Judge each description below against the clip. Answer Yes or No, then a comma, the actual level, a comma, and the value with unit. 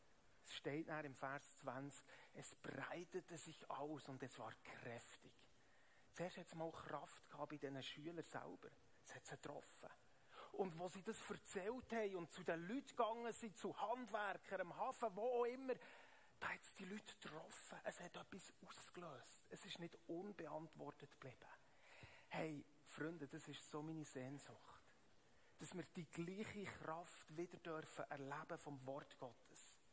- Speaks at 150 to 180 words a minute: Yes, average, 160 wpm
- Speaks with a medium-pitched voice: Yes, medium, 165 Hz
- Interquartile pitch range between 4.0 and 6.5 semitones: Yes, average, 4.6 semitones